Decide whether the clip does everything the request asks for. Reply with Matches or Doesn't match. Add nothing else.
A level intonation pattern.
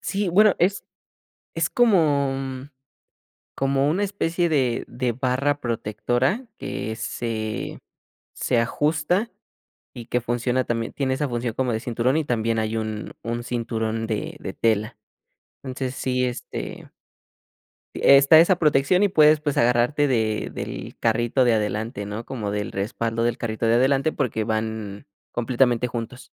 Doesn't match